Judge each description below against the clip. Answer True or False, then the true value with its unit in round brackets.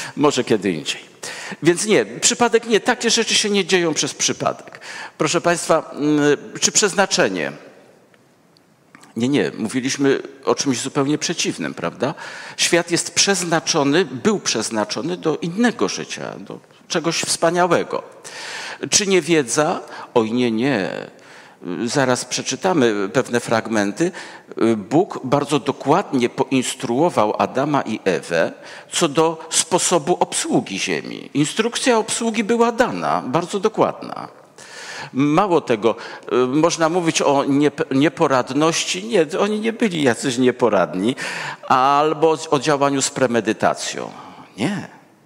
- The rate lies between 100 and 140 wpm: True (110 wpm)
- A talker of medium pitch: True (160 Hz)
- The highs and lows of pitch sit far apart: True (6.1 semitones)